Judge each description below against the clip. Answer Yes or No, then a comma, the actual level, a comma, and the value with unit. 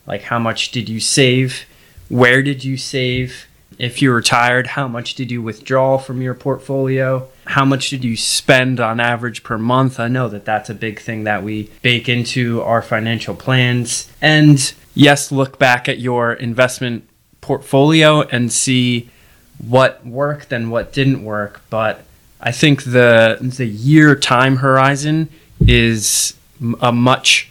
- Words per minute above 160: No, average, 155 wpm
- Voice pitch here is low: Yes, low, 125 Hz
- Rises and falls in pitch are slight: Yes, narrow, 2.3 semitones